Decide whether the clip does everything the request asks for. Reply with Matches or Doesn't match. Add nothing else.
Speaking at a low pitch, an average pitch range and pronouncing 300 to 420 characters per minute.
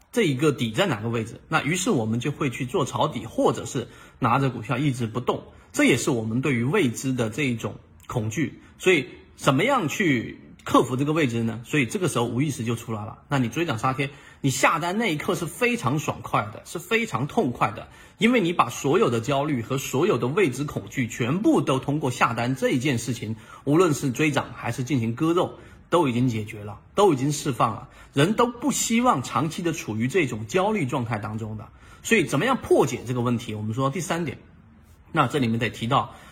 Matches